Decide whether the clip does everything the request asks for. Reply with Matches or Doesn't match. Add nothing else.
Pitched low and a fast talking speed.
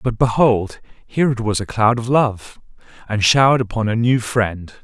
Doesn't match